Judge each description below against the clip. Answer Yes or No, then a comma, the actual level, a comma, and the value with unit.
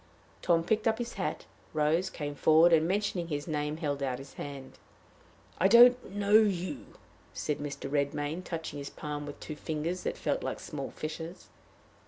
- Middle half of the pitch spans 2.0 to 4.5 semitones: Yes, average, 4.1 semitones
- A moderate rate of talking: Yes, average, 170 wpm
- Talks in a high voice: No, medium, 160 Hz